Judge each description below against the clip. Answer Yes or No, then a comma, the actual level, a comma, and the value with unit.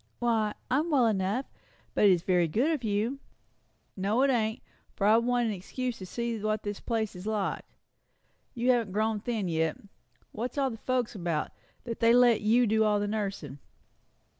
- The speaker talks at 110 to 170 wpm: No, average, 180 wpm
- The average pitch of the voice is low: No, high, 220 Hz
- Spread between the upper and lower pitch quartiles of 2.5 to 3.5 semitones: Yes, average, 3.1 semitones